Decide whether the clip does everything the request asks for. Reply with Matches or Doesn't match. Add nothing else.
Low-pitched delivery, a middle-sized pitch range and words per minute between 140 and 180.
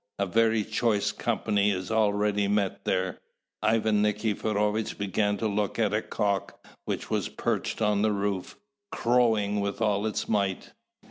Doesn't match